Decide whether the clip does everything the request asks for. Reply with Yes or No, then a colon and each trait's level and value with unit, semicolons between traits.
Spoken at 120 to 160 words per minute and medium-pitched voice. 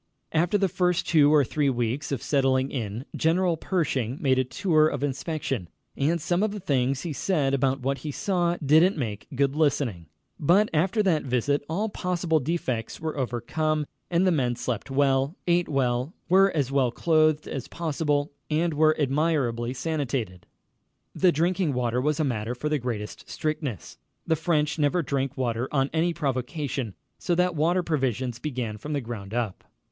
No: average, 170 wpm; medium, 145 Hz